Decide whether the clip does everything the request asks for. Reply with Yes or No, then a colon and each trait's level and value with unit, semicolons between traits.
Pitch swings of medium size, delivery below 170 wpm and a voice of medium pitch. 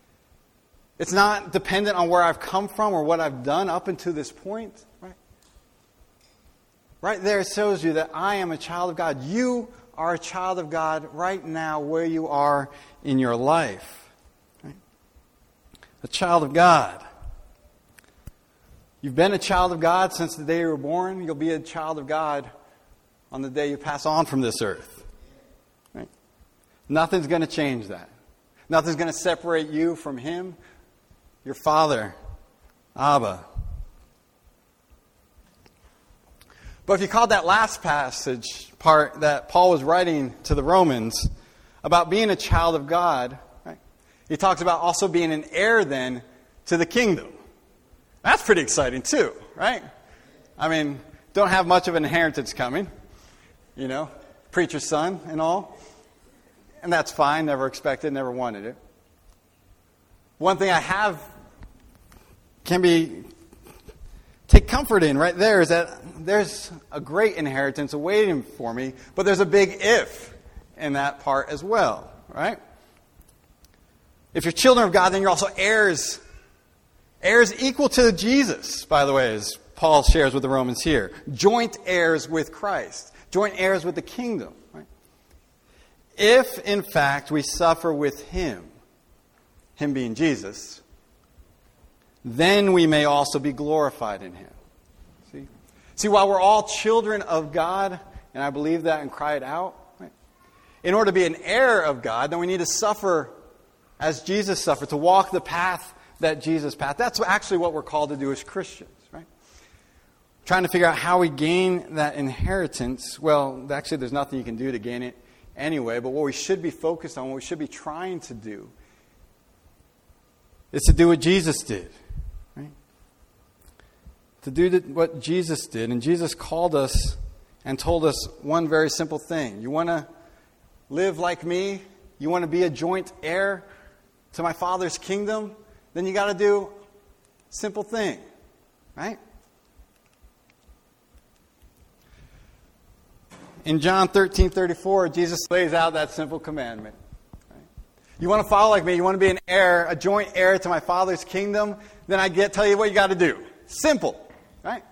Yes: average, 5.0 semitones; average, 160 wpm; medium, 165 Hz